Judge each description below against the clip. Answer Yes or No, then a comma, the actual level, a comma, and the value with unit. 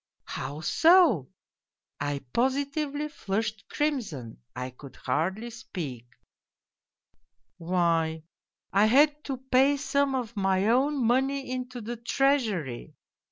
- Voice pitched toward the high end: Yes, high, 230 Hz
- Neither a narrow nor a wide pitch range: No, wide, 8.7 semitones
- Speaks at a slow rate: Yes, slow, 115 wpm